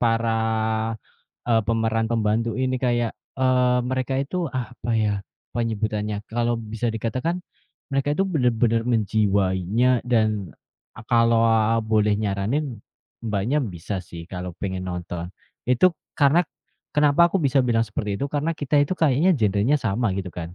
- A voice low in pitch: Yes, low, 115 Hz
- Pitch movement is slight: No, average, 3.5 semitones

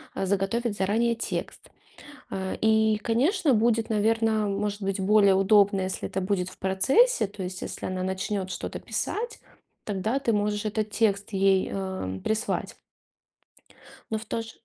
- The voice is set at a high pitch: Yes, high, 205 Hz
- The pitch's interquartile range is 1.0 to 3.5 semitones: Yes, narrow, 2.6 semitones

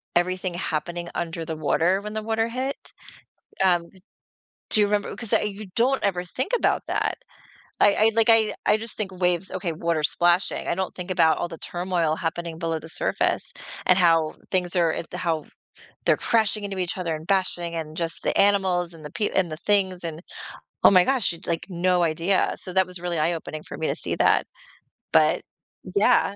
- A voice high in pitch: No, medium, 180 Hz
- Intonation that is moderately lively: Yes, average, 3.1 semitones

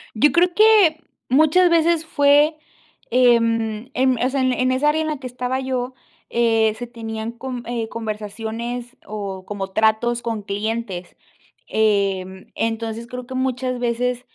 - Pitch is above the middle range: Yes, high, 240 Hz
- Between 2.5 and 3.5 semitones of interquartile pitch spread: Yes, average, 3.0 semitones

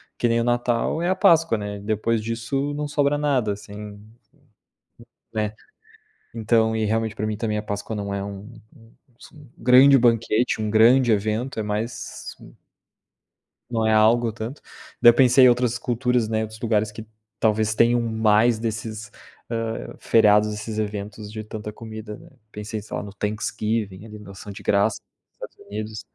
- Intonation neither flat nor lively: No, narrow, 1.9 semitones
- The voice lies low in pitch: Yes, low, 110 Hz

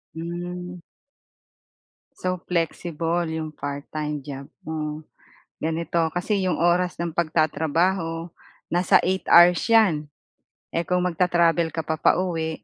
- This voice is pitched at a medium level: Yes, medium, 170 Hz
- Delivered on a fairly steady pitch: Yes, narrow, 2.0 semitones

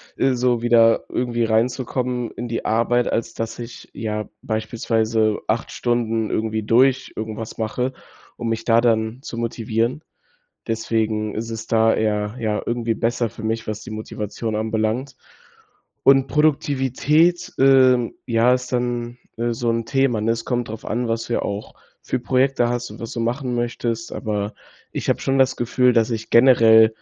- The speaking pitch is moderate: No, low, 115 Hz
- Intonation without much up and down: Yes, narrow, 1.8 semitones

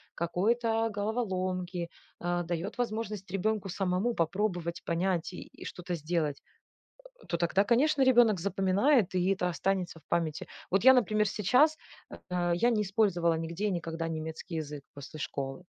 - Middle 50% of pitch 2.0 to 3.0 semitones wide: No, average, 3.9 semitones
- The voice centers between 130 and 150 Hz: No, medium, 185 Hz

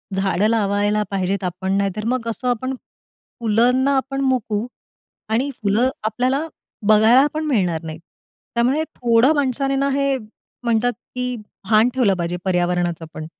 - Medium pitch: No, high, 230 Hz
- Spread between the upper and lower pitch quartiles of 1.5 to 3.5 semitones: No, average, 4.6 semitones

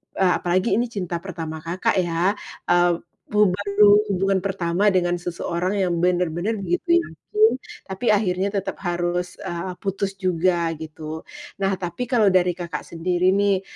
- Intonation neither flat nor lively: No, narrow, 2.3 semitones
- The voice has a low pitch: No, medium, 185 Hz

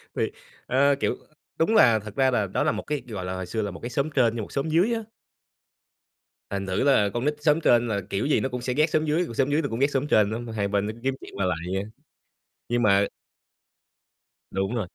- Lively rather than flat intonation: Yes, wide, 5.7 semitones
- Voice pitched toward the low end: Yes, low, 120 Hz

